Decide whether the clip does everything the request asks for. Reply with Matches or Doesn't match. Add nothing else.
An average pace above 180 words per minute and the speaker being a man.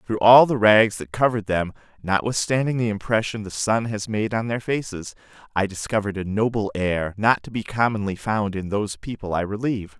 Matches